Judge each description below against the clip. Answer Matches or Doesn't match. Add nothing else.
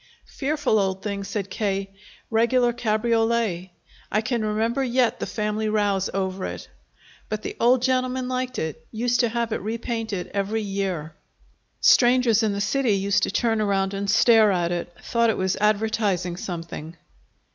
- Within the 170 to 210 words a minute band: Doesn't match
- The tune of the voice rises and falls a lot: Doesn't match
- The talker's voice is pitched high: Matches